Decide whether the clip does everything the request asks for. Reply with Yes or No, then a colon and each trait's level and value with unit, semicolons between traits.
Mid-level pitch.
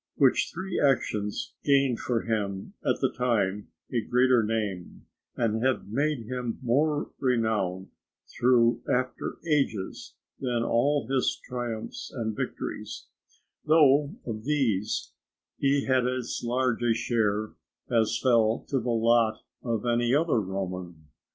No: low, 120 Hz